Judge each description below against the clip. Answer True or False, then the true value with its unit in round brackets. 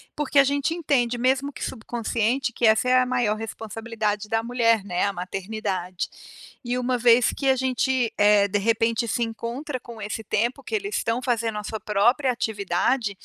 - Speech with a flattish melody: False (3.0 semitones)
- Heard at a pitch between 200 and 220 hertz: False (230 Hz)